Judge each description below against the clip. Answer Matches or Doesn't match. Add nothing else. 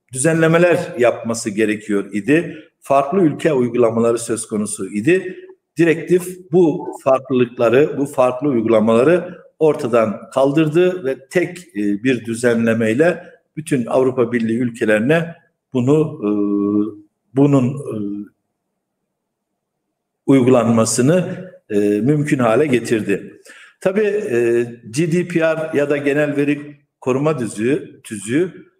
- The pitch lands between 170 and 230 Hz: Doesn't match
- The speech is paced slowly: Matches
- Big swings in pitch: Matches